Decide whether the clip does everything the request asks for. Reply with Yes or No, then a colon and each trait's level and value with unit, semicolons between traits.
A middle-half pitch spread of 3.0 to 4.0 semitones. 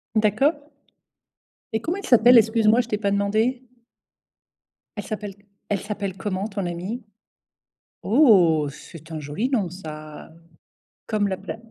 Yes: average, 3.7 semitones